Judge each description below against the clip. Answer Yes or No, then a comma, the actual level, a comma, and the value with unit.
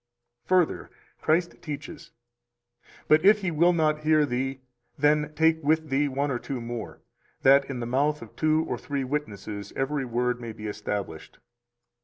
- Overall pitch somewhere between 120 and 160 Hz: Yes, medium, 140 Hz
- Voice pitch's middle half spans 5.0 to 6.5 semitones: No, average, 4.0 semitones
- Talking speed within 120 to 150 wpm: No, average, 165 wpm